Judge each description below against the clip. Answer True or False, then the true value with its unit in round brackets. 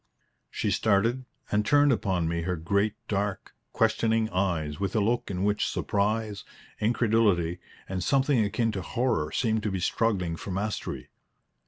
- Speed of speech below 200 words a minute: True (150 wpm)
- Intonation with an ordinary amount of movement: True (3.5 semitones)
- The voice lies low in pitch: True (105 Hz)